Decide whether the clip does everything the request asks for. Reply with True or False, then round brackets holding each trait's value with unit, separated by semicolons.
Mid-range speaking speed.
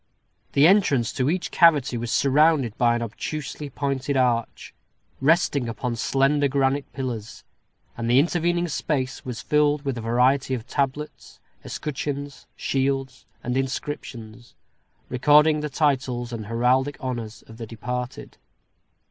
False (130 wpm)